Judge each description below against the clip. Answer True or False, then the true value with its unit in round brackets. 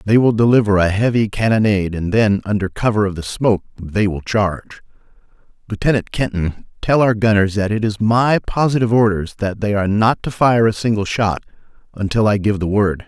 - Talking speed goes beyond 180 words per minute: True (190 wpm)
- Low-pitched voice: True (105 Hz)